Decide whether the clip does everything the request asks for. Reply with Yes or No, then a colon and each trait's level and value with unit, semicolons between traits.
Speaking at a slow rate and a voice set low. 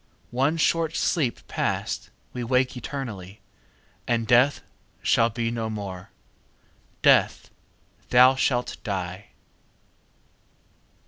Yes: slow, 90 wpm; low, 120 Hz